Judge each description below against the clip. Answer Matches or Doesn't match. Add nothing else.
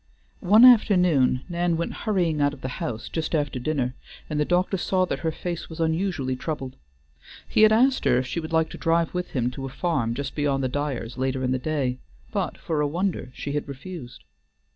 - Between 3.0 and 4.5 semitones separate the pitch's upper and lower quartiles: Doesn't match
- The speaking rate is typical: Doesn't match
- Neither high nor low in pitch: Matches